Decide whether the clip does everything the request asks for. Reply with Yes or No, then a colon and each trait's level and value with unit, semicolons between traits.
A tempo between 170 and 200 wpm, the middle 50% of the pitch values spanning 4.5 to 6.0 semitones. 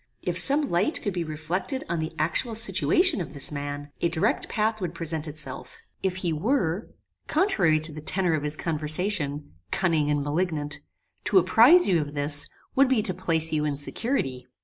Yes: average, 180 wpm; average, 5.1 semitones